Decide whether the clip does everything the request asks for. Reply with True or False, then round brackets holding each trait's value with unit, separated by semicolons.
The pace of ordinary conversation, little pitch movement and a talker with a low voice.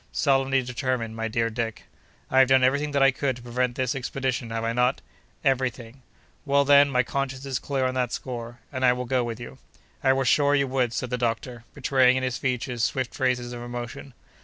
False (220 wpm; 1.8 semitones; 130 Hz)